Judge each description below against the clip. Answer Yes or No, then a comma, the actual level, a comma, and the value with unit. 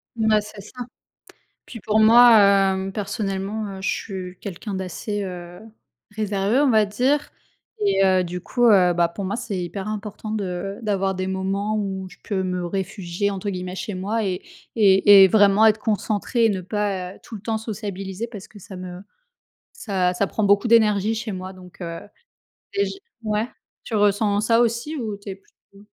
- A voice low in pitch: No, high, 200 Hz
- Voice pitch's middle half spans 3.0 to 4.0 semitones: No, narrow, 2.4 semitones